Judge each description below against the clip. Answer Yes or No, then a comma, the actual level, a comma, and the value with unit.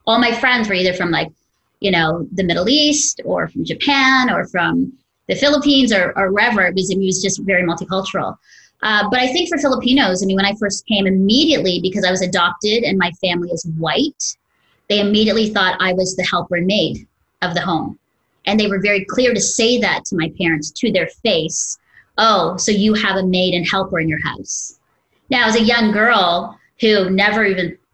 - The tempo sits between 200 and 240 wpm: Yes, fast, 205 wpm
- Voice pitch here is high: Yes, high, 200 Hz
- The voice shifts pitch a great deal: No, average, 4.2 semitones